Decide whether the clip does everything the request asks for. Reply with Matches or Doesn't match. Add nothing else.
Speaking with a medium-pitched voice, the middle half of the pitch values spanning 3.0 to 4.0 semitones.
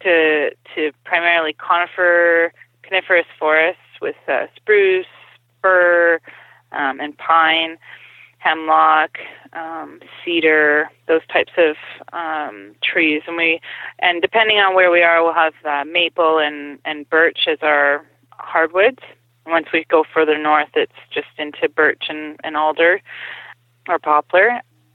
Doesn't match